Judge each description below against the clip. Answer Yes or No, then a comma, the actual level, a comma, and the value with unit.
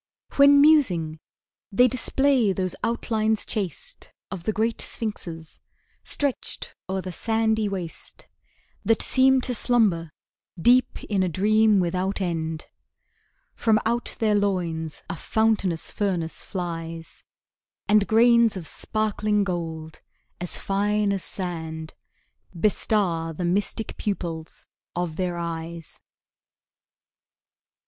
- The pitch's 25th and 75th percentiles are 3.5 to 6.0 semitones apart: Yes, average, 4.6 semitones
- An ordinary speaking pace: No, slow, 110 wpm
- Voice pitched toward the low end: No, high, 195 Hz